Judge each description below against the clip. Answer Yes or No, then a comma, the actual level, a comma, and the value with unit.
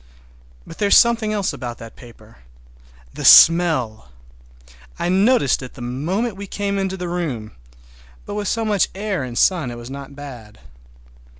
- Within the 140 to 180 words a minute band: Yes, average, 160 wpm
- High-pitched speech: No, medium, 155 Hz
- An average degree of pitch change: No, wide, 8.9 semitones